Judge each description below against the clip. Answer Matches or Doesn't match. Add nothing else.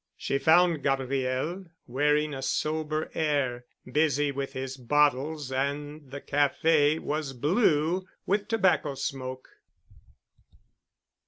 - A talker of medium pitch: Matches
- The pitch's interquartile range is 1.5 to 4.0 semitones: Matches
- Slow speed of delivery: Matches